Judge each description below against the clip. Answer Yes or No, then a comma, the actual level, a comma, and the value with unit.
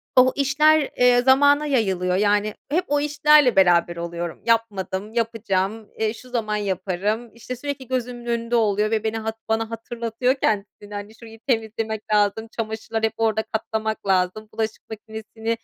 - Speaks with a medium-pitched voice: No, high, 220 Hz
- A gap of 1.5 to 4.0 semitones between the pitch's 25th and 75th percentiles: Yes, narrow, 2.6 semitones